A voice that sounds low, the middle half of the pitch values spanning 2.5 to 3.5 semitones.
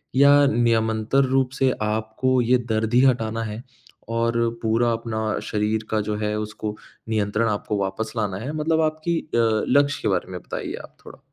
Yes: low, 115 Hz; average, 3.2 semitones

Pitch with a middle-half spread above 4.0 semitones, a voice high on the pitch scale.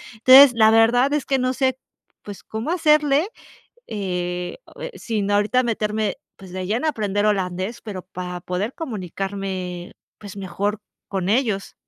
Yes: average, 4.6 semitones; high, 210 Hz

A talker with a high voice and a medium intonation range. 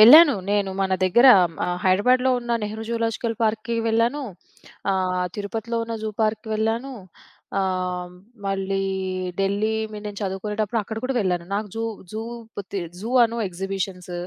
Yes: high, 210 Hz; average, 3.0 semitones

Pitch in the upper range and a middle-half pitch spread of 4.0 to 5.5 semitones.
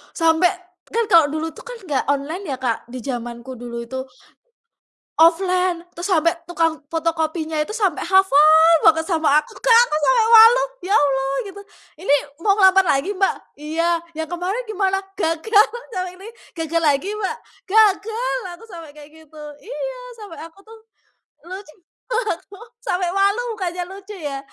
Yes: very high, 345 Hz; average, 4.4 semitones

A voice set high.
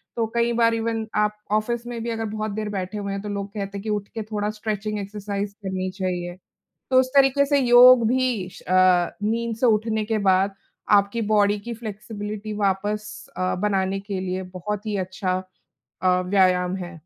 Yes: high, 210 Hz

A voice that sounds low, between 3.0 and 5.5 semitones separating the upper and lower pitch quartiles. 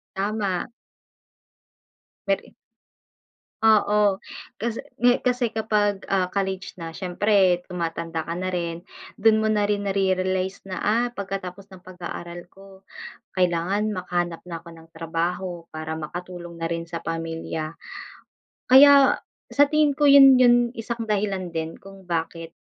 No: medium, 185 Hz; average, 3.5 semitones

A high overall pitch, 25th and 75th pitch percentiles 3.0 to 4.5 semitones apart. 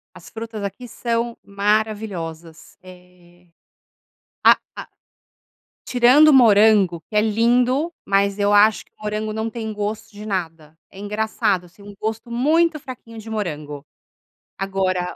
Yes: high, 210 Hz; average, 3.3 semitones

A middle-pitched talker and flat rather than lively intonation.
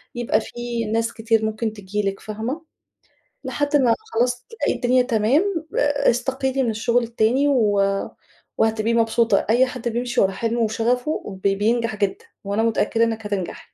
No: high, 230 Hz; narrow, 2.3 semitones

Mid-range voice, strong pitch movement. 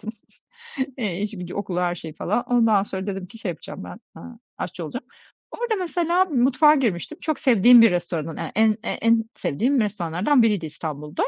No: high, 210 Hz; wide, 5.8 semitones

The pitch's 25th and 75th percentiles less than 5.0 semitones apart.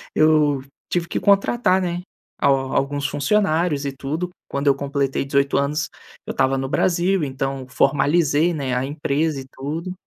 Yes: average, 3.5 semitones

